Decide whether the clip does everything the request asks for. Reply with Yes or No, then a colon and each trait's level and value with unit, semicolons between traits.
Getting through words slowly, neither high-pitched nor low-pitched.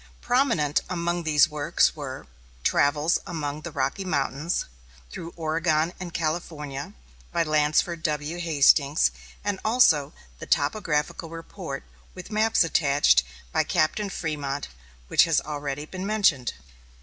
Yes: slow, 120 wpm; medium, 155 Hz